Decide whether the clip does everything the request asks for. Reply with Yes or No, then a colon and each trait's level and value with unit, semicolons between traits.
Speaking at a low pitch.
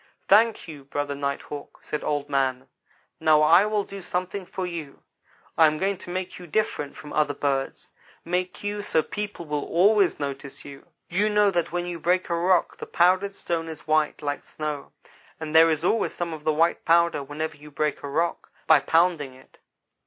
No: medium, 160 Hz